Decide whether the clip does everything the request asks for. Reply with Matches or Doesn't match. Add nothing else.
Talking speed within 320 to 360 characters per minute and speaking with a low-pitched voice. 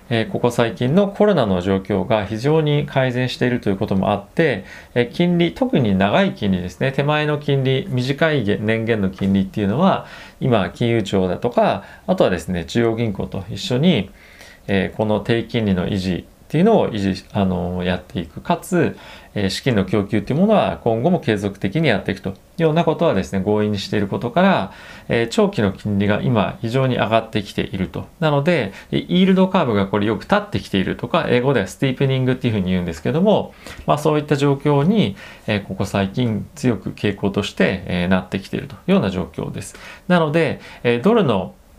Doesn't match